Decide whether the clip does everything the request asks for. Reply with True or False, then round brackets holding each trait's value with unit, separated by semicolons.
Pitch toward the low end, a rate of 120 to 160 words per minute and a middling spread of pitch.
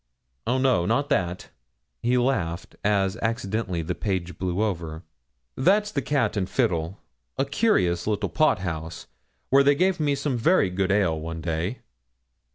False (100 Hz; 155 wpm; 7.5 semitones)